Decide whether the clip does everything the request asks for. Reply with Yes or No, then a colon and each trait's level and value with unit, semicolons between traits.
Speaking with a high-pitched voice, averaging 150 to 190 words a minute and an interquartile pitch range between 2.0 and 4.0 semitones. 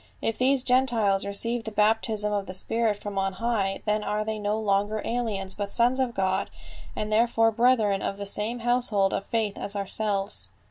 Yes: high, 215 Hz; average, 185 wpm; narrow, 2.5 semitones